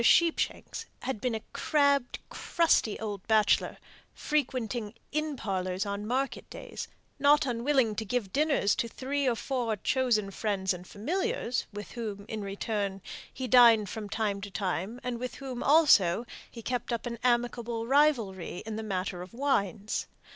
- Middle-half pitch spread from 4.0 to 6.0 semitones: Yes, average, 4.3 semitones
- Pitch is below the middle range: No, high, 230 Hz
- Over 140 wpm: Yes, average, 155 wpm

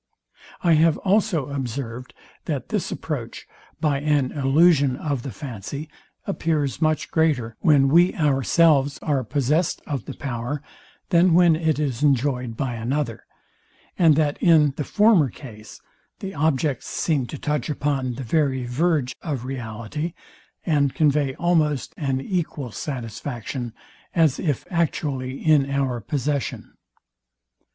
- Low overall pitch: No, medium, 145 Hz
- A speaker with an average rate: No, slow, 130 wpm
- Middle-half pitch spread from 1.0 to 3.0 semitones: No, average, 3.4 semitones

